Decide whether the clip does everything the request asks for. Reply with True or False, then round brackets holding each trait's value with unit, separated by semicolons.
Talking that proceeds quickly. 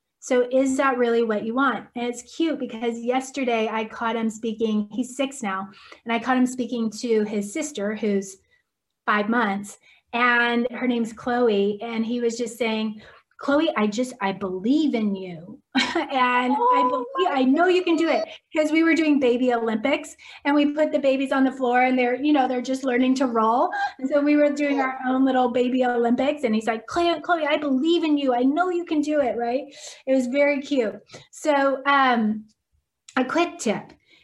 False (195 wpm)